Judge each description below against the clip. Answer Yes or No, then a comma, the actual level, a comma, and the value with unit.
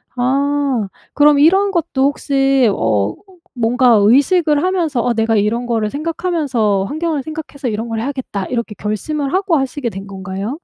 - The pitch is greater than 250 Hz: Yes, very high, 265 Hz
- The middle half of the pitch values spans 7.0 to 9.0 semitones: No, average, 5.2 semitones